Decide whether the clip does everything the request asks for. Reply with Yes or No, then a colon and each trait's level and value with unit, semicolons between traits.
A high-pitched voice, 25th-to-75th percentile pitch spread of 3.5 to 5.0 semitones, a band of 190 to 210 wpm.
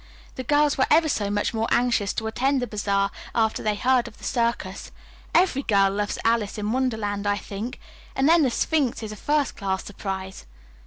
Yes: high, 220 Hz; average, 4.3 semitones; average, 195 wpm